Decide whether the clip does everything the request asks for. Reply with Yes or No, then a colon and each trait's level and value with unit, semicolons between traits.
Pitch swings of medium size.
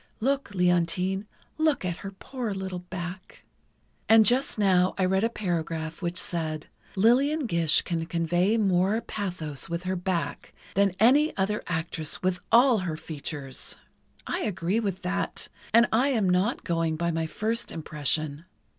Yes: average, 4.2 semitones